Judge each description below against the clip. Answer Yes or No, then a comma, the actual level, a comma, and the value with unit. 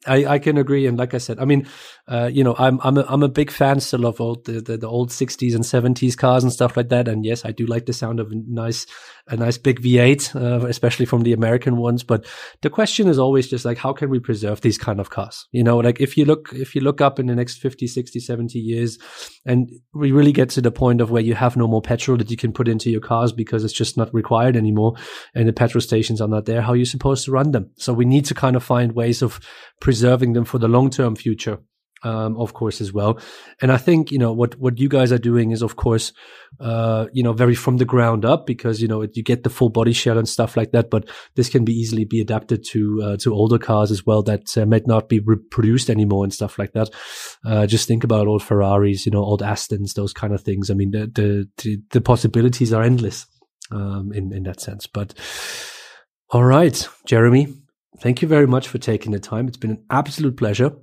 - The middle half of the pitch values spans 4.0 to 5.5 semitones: No, narrow, 2.4 semitones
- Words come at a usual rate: No, fast, 250 wpm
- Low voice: Yes, low, 120 Hz